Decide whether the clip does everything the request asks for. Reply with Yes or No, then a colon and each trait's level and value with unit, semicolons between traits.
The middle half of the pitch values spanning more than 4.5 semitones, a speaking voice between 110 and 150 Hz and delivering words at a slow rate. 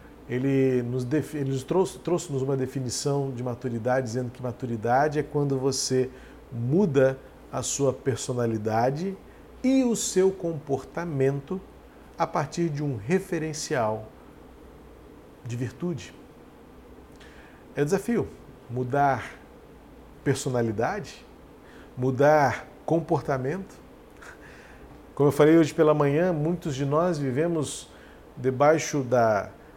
No: average, 3.5 semitones; medium, 140 Hz; slow, 95 wpm